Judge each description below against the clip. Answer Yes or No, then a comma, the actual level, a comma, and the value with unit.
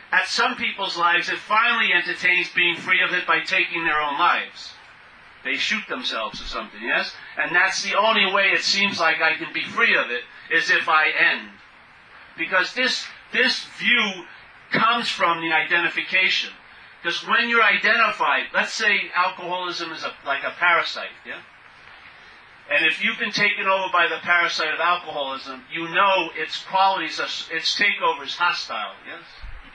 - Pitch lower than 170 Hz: No, medium, 180 Hz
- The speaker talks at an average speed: Yes, average, 165 wpm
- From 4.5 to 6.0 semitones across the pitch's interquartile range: No, average, 3.3 semitones